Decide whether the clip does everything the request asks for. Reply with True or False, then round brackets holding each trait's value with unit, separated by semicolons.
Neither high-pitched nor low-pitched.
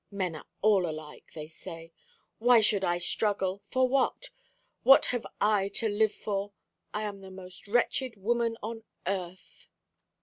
False (205 Hz)